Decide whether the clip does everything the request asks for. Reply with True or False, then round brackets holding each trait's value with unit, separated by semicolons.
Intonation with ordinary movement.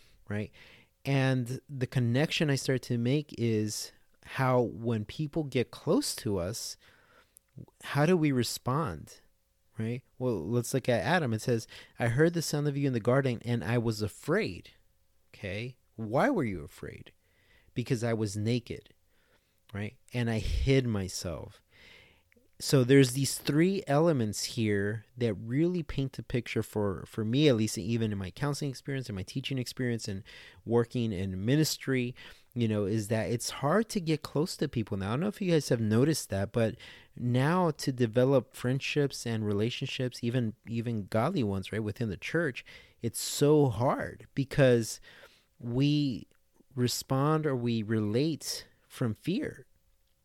True (3.9 semitones)